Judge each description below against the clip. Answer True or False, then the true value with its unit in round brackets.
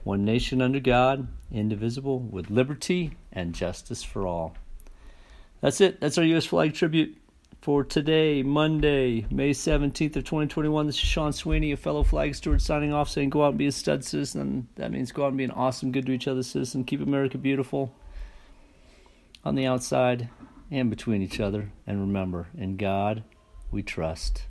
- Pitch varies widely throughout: True (7.1 semitones)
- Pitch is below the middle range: True (125 Hz)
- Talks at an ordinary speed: True (175 wpm)